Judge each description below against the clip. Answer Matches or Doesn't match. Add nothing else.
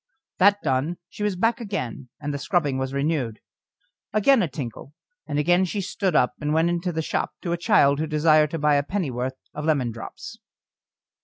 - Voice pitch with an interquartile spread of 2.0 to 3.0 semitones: Doesn't match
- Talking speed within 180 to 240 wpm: Matches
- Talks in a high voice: Doesn't match